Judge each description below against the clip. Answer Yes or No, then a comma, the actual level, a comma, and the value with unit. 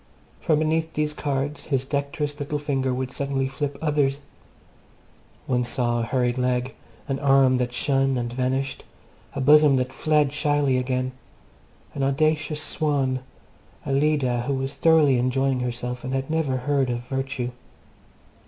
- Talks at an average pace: Yes, average, 145 wpm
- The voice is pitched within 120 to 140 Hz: Yes, low, 135 Hz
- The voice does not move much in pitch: Yes, narrow, 2.3 semitones